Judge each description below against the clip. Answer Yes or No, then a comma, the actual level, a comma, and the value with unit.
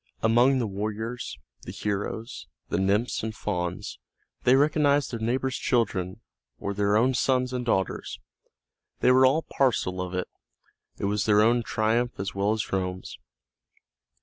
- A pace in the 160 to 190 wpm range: No, average, 150 wpm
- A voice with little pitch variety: No, average, 4.0 semitones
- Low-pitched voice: Yes, low, 110 Hz